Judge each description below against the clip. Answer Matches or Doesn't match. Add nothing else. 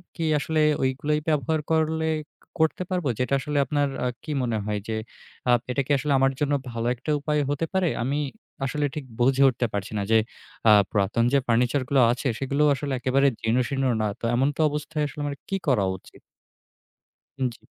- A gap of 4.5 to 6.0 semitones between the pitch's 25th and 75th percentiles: Doesn't match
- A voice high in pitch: Doesn't match